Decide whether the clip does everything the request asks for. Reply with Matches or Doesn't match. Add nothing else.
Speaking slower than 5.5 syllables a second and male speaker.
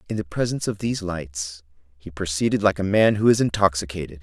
Doesn't match